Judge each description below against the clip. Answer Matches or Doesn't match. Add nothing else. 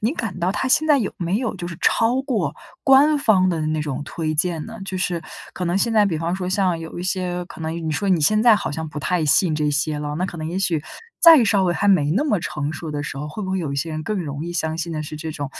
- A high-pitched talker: Doesn't match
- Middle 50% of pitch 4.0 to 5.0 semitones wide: Matches